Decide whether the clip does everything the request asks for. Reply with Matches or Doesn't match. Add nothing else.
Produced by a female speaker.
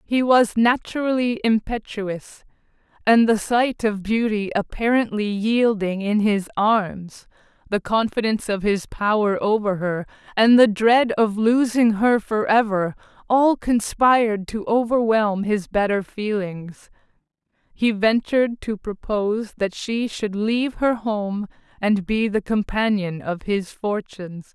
Matches